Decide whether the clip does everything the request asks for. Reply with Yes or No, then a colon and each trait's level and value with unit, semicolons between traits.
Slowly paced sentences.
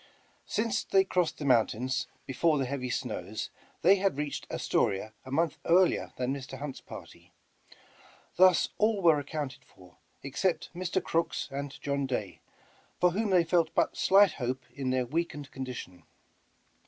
No: average, 155 wpm